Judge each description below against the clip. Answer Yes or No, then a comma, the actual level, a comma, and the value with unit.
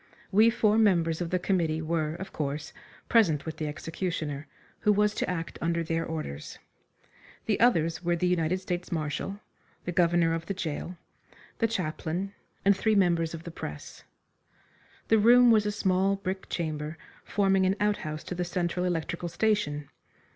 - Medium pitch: Yes, medium, 175 Hz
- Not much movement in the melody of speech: No, average, 3.5 semitones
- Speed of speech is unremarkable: Yes, average, 160 wpm